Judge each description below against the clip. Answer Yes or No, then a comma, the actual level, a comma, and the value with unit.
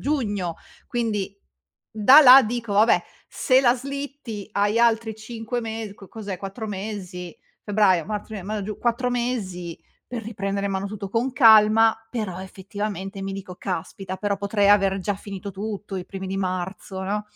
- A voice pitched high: Yes, high, 205 Hz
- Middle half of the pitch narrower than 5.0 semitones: Yes, average, 2.7 semitones